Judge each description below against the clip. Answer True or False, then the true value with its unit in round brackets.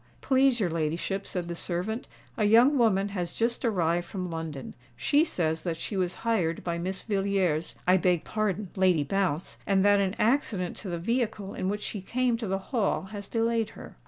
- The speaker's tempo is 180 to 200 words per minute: True (185 wpm)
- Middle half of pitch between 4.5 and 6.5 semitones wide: False (4.1 semitones)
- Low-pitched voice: False (195 Hz)